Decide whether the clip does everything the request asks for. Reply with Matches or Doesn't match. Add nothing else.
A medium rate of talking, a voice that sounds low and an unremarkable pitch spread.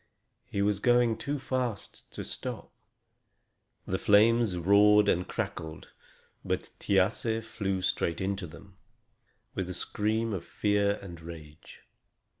Doesn't match